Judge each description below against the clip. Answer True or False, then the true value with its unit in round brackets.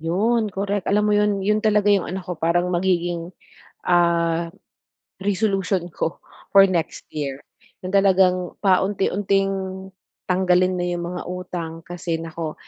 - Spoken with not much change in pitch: True (2.3 semitones)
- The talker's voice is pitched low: False (180 Hz)